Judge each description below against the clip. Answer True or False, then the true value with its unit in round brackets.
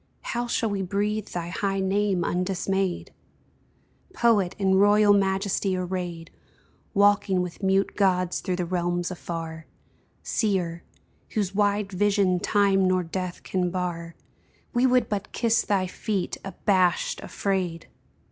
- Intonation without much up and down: True (2.2 semitones)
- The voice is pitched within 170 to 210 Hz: True (190 Hz)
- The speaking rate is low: True (125 wpm)